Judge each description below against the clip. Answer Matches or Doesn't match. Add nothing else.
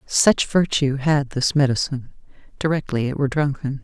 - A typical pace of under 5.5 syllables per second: Matches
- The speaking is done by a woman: Matches